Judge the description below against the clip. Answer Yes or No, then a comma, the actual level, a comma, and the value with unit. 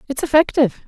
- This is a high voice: Yes, very high, 280 Hz